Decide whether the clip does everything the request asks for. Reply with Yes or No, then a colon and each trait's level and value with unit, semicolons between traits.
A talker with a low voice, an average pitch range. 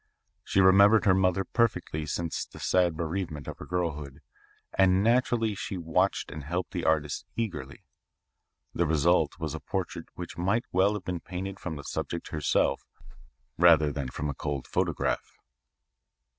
Yes: very low, 90 Hz; average, 3.9 semitones